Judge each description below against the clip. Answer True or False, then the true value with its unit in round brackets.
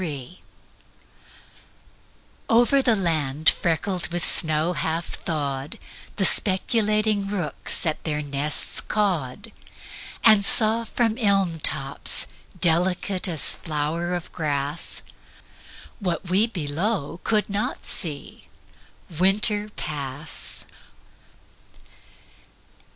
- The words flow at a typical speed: False (90 wpm)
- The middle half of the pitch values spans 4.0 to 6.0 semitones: True (5.2 semitones)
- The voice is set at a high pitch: False (175 Hz)